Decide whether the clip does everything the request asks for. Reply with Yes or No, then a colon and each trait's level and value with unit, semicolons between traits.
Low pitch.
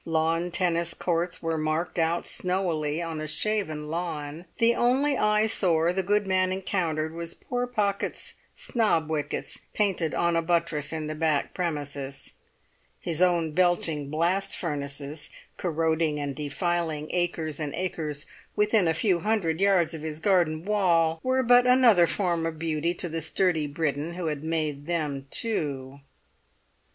No: medium, 165 Hz